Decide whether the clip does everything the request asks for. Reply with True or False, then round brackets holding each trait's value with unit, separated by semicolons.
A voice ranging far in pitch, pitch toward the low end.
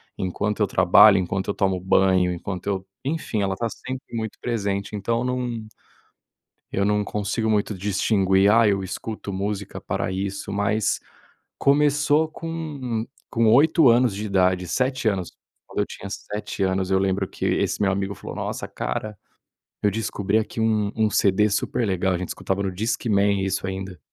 False (2.8 semitones; 100 Hz)